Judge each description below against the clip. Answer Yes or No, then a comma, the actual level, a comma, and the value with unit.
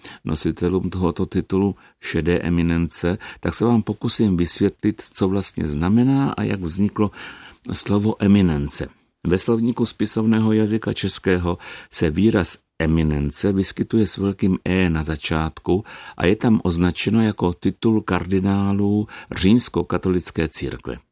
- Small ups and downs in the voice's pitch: No, average, 3.7 semitones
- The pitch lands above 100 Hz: No, very low, 95 Hz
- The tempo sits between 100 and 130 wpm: Yes, slow, 115 wpm